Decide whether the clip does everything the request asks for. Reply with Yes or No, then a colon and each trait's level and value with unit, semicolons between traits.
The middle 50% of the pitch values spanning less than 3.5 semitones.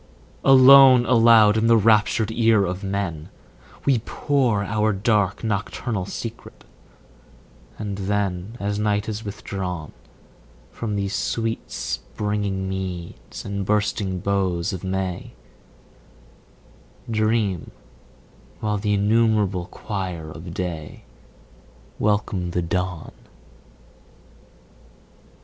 Yes: average, 2.8 semitones